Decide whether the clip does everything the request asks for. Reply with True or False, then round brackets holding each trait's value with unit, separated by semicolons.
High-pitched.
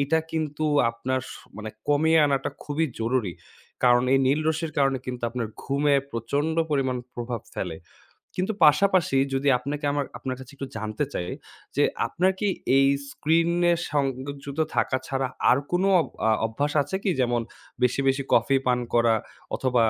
False (135 Hz)